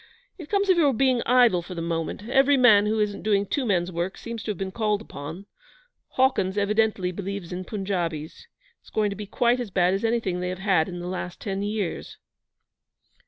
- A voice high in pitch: Yes, high, 200 Hz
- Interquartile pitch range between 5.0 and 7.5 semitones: No, average, 4.1 semitones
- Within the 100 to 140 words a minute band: No, fast, 205 wpm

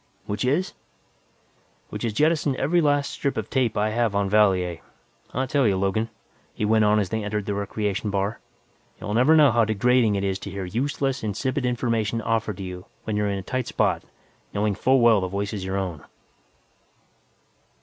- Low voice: Yes, low, 110 Hz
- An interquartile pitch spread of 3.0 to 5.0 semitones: Yes, average, 3.9 semitones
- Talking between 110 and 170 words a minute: No, average, 190 wpm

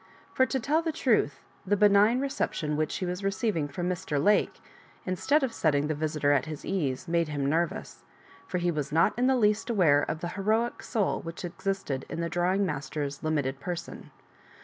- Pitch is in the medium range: Yes, medium, 175 Hz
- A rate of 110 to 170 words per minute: No, average, 190 wpm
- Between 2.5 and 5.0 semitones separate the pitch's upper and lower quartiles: No, wide, 5.6 semitones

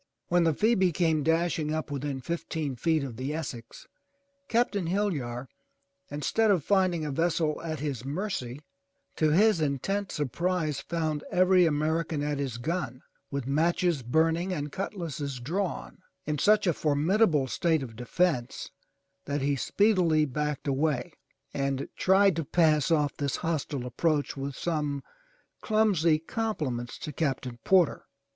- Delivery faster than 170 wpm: No, average, 140 wpm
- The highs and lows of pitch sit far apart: No, average, 3.9 semitones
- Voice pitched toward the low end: No, medium, 155 Hz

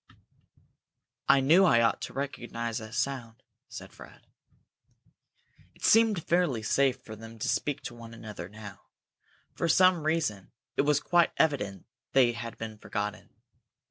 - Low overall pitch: Yes, low, 120 Hz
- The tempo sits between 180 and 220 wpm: No, average, 140 wpm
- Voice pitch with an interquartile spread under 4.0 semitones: No, average, 5.1 semitones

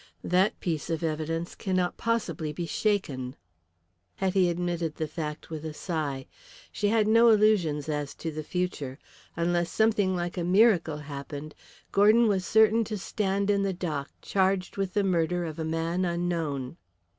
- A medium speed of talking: Yes, average, 155 wpm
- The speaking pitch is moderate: Yes, medium, 175 Hz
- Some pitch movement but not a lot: Yes, average, 3.9 semitones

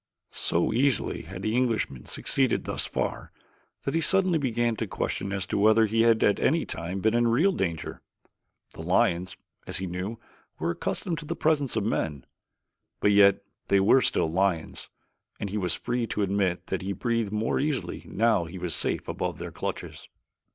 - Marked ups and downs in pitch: No, average, 4.4 semitones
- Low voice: Yes, low, 105 Hz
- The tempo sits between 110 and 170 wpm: No, average, 185 wpm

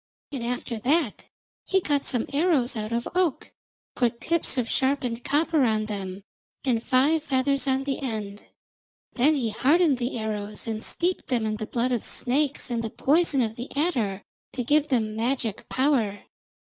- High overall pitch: Yes, very high, 250 Hz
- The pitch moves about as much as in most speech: Yes, average, 4.3 semitones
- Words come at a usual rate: Yes, average, 170 wpm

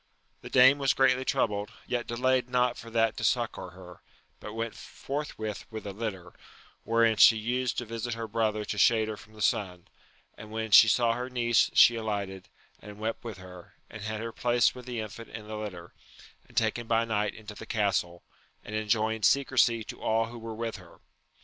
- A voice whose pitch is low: Yes, low, 110 Hz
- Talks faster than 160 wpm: Yes, average, 195 wpm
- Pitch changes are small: Yes, narrow, 2.0 semitones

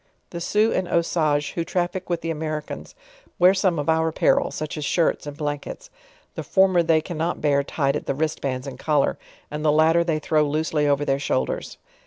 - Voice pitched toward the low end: No, medium, 155 Hz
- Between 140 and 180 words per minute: No, average, 200 wpm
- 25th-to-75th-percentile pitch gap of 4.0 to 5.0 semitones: No, narrow, 2.6 semitones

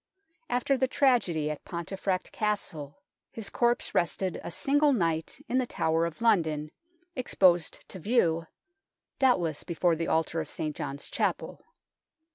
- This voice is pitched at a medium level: Yes, medium, 175 Hz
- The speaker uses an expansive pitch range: Yes, wide, 6.7 semitones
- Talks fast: No, slow, 135 wpm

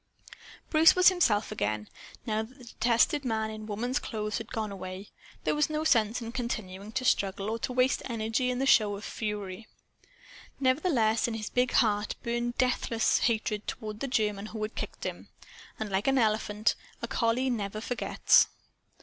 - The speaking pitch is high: Yes, high, 225 Hz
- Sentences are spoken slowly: No, average, 175 wpm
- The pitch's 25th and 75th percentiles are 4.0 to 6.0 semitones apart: No, average, 2.9 semitones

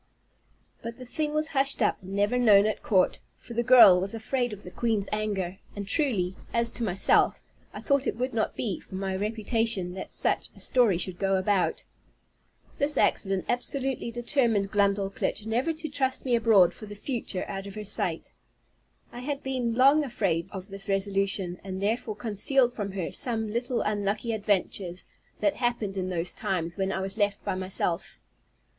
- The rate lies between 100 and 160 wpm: No, average, 180 wpm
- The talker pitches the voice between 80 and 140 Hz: No, high, 210 Hz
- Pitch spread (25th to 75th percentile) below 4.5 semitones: Yes, average, 3.9 semitones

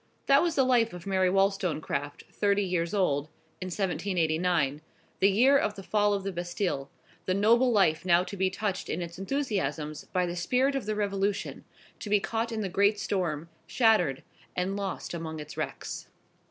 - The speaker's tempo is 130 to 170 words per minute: No, average, 180 wpm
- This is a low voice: No, high, 190 Hz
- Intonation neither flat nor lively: Yes, average, 3.4 semitones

